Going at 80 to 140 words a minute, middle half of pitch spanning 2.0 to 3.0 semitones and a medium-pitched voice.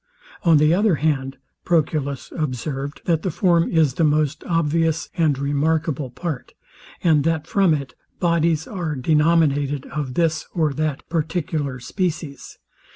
Yes: slow, 135 wpm; average, 2.7 semitones; medium, 155 Hz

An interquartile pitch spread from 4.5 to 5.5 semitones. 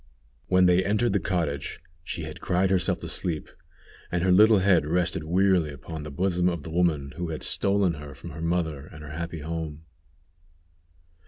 No: average, 3.2 semitones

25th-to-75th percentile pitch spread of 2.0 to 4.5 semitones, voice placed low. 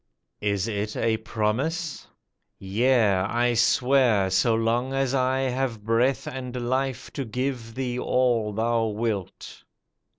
Yes: average, 3.0 semitones; low, 120 Hz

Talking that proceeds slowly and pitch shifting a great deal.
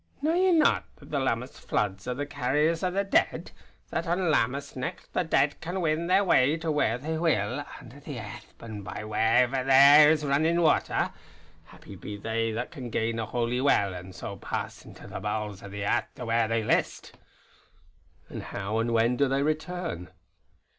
No: average, 190 wpm; wide, 5.8 semitones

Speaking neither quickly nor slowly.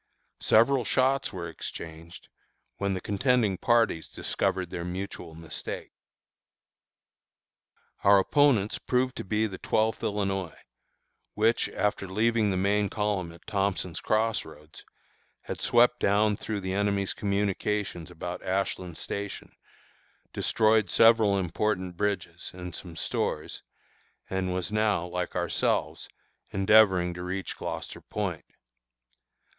No: slow, 115 wpm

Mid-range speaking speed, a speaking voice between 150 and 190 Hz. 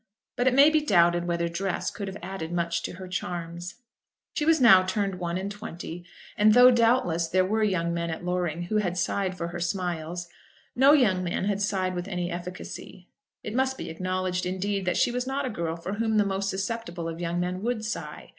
No: fast, 210 wpm; medium, 185 Hz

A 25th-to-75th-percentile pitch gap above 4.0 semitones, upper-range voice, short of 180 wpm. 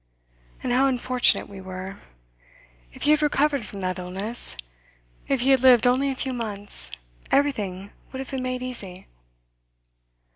Yes: average, 5.2 semitones; high, 245 Hz; average, 150 wpm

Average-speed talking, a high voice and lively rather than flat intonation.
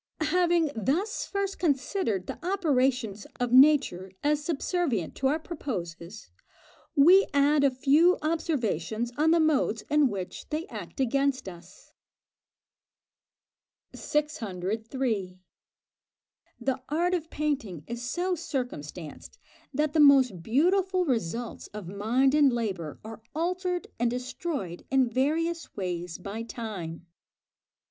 No: slow, 115 wpm; very high, 265 Hz; wide, 6.7 semitones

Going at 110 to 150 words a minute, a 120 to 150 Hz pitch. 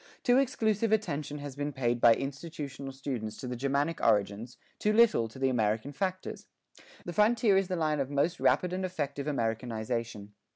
No: average, 170 wpm; medium, 140 Hz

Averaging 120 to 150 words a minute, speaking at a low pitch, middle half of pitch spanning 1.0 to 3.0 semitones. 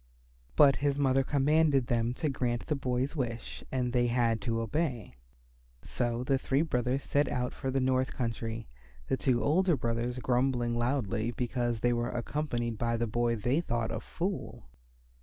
No: average, 165 wpm; low, 125 Hz; narrow, 2.5 semitones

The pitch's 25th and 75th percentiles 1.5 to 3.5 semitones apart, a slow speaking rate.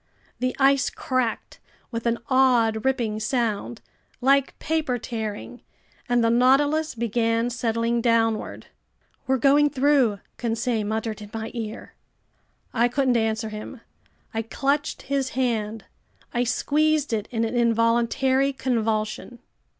Yes: average, 2.9 semitones; slow, 120 wpm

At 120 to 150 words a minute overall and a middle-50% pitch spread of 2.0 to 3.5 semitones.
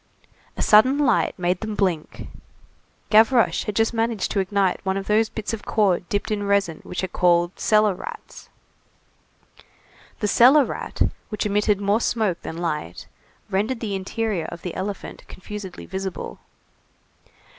Yes: average, 145 wpm; average, 2.8 semitones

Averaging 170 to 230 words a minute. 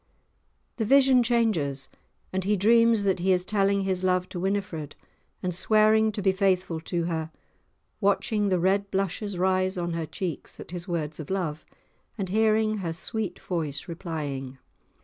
No: average, 160 wpm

